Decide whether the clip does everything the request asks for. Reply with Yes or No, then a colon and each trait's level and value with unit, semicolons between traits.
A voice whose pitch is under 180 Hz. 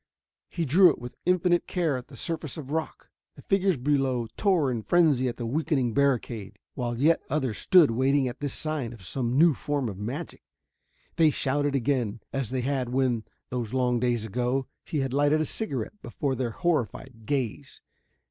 Yes: low, 135 Hz